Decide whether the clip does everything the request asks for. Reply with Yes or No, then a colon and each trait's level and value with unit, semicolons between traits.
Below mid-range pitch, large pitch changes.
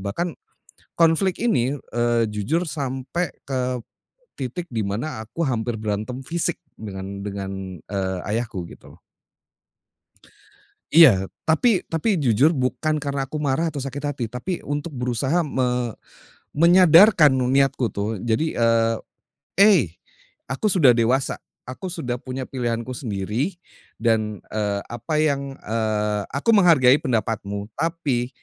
Yes: low, 130 Hz; wide, 5.9 semitones